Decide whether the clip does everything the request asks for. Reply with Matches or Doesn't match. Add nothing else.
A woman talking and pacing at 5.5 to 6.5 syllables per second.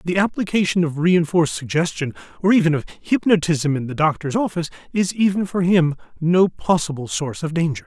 Doesn't match